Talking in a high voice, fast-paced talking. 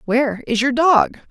No: very high, 260 Hz; average, 185 wpm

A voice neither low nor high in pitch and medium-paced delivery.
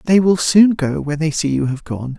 No: medium, 150 Hz; fast, 275 wpm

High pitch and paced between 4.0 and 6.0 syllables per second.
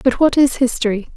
Yes: very high, 250 Hz; 5.9 syllables/s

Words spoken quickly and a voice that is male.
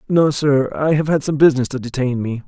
Yes: fast, 240 wpm; male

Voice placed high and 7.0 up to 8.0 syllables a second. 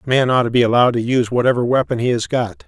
No: low, 120 Hz; 7.5 syllables/s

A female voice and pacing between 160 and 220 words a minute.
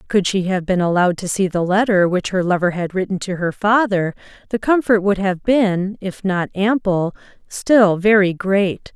Yes: female; average, 190 wpm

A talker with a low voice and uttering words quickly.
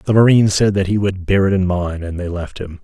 Yes: very low, 95 Hz; fast, 295 wpm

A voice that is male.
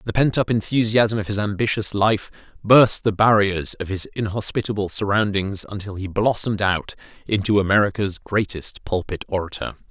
Yes: male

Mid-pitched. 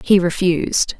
Yes: medium, 180 Hz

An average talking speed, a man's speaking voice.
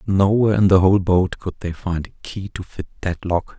No: fast, 250 wpm; male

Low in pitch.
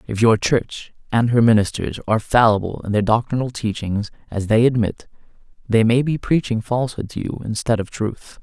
Yes: low, 115 Hz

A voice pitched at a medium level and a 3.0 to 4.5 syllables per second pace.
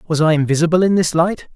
No: medium, 165 Hz; 6.0 syllables/s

